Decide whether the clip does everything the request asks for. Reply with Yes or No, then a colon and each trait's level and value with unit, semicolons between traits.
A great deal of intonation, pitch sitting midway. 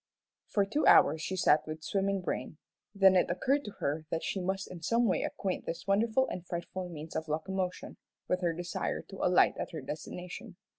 No: average, 3.1 semitones; medium, 180 Hz